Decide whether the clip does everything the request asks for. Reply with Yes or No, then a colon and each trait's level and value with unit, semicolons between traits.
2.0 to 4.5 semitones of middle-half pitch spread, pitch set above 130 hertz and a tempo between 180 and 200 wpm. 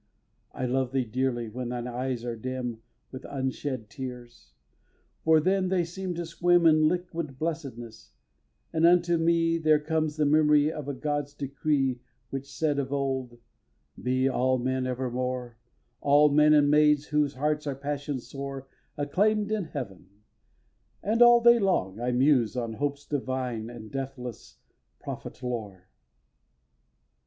No: average, 3.5 semitones; medium, 140 Hz; average, 145 wpm